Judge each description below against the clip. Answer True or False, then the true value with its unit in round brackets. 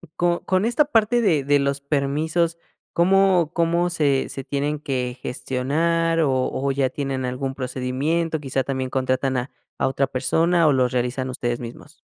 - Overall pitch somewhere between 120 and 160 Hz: True (140 Hz)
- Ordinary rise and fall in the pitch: True (4.2 semitones)